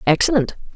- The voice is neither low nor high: No, high, 205 Hz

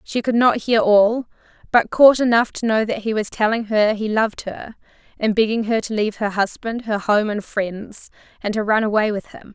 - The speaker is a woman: Yes, female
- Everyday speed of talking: No, fast, 220 wpm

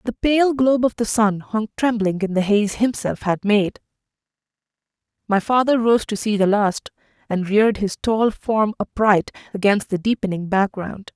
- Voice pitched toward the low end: No, high, 210 Hz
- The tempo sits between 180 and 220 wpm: No, average, 165 wpm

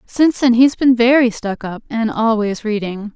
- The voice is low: No, high, 230 Hz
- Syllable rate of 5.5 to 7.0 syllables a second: No, 4.7 syllables/s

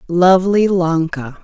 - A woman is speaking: Yes, female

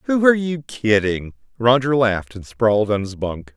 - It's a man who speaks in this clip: Yes, male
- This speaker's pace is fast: No, average, 185 wpm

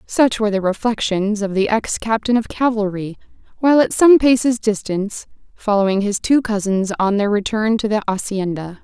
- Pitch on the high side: Yes, high, 215 Hz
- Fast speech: No, average, 170 wpm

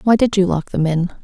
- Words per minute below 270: No, fast, 290 wpm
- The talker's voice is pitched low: No, high, 190 Hz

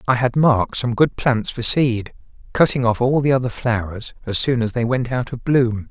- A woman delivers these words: No, male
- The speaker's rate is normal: No, fast, 225 wpm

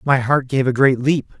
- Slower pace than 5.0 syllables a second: Yes, 4.8 syllables/s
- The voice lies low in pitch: Yes, low, 130 Hz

